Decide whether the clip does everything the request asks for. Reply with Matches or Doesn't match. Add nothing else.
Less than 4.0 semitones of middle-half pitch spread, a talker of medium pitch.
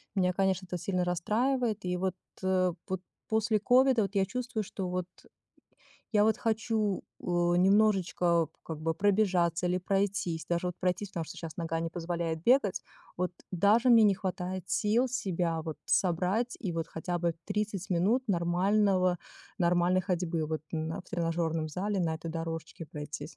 Matches